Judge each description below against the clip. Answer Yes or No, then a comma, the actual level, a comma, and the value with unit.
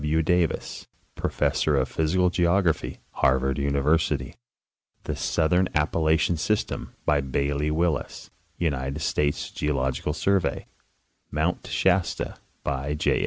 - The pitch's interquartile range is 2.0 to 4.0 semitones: Yes, average, 3.4 semitones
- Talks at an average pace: No, slow, 110 wpm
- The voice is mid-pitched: No, very low, 75 Hz